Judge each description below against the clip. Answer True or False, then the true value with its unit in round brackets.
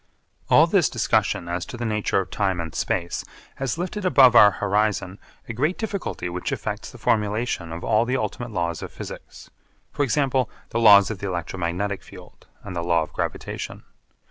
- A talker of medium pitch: False (105 Hz)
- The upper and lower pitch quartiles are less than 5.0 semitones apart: False (5.6 semitones)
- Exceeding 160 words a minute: True (180 wpm)